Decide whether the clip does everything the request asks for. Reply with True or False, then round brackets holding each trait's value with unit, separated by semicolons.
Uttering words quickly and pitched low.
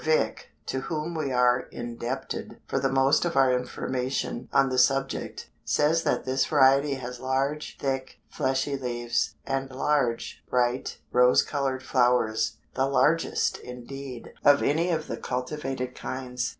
False (140 wpm; 130 Hz)